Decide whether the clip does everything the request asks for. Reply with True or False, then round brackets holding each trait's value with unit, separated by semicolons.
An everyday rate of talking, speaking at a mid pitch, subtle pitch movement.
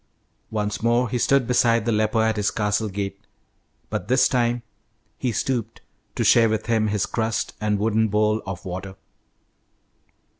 False (155 wpm; 110 Hz; 2.0 semitones)